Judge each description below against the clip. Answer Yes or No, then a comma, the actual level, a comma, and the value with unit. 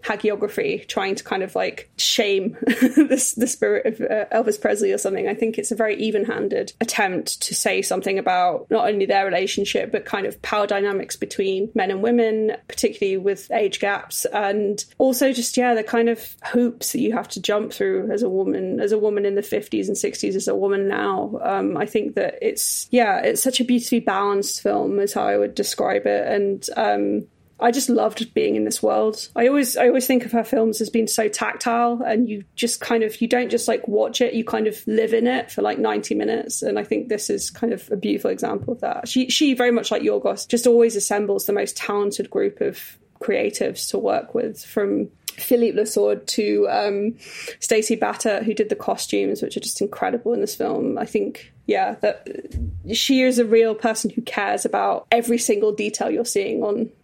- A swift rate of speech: Yes, fast, 210 wpm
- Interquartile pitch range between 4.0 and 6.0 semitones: No, average, 3.1 semitones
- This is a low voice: No, high, 225 Hz